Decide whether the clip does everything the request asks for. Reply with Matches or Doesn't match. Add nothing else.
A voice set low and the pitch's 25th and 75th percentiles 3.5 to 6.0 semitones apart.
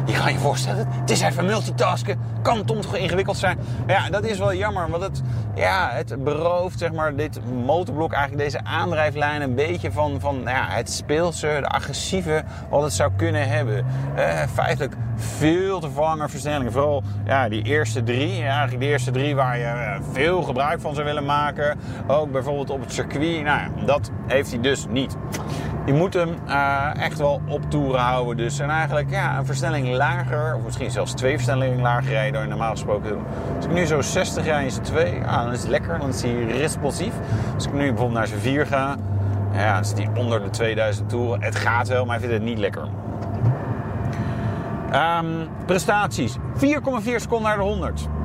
Matches